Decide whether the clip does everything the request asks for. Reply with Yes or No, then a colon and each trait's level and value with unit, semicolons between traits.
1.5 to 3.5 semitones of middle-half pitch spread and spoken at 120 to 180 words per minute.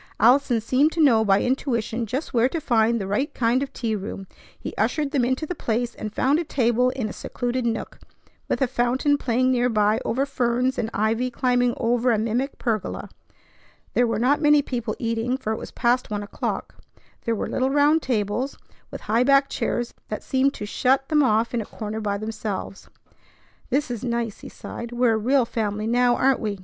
No: average, 2.9 semitones; average, 200 wpm